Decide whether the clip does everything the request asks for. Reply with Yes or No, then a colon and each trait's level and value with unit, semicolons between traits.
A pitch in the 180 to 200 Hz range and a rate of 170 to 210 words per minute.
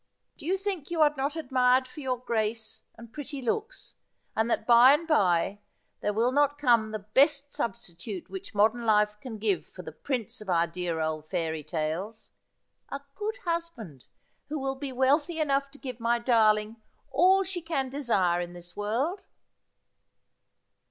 No: high, 240 Hz; average, 175 wpm